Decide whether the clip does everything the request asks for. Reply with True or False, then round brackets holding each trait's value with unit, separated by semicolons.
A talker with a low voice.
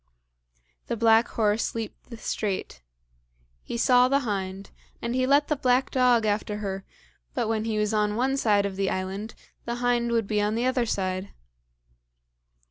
False (225 Hz)